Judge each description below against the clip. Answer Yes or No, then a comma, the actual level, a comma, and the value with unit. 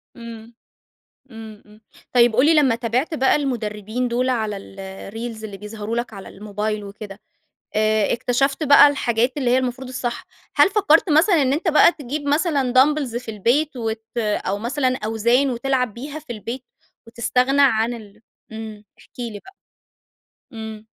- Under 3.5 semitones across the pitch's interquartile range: No, average, 3.8 semitones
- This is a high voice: Yes, high, 240 Hz